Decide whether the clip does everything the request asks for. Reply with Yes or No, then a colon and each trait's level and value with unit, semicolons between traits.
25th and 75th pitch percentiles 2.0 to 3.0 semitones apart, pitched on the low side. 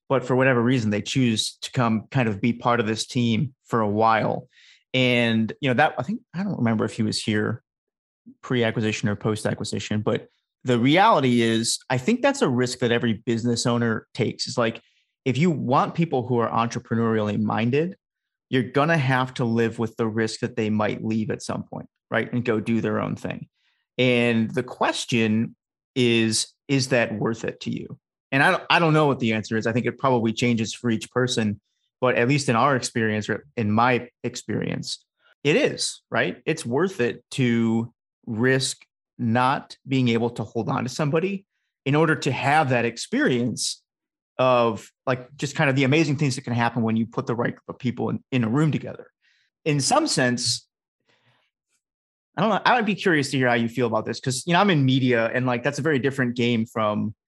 Yes: average, 2.7 semitones; low, 120 Hz